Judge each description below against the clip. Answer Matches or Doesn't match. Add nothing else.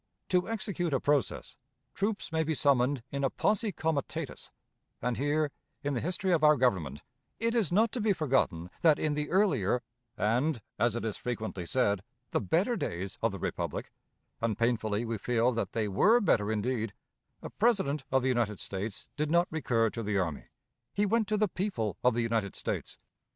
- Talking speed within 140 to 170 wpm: Doesn't match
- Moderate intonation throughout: Doesn't match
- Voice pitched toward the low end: Matches